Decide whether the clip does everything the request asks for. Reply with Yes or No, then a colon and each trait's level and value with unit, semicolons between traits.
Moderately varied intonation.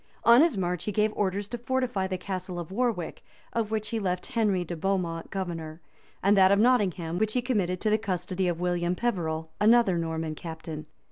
Yes: average, 3.8 semitones